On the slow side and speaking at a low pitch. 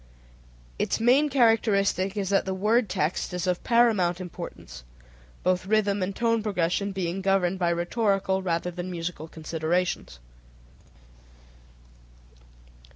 No: slow, 120 wpm; high, 190 Hz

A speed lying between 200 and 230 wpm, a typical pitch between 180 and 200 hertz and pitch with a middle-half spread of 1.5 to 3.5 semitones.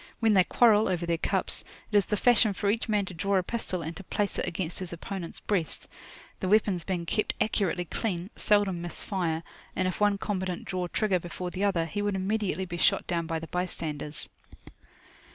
Yes: fast, 205 wpm; medium, 185 Hz; average, 3.1 semitones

